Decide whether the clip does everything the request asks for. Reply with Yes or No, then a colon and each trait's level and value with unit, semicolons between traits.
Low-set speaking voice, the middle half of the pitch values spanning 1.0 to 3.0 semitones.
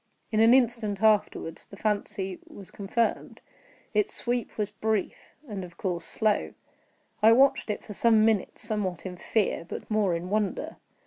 No: high, 210 Hz; narrow, 2.4 semitones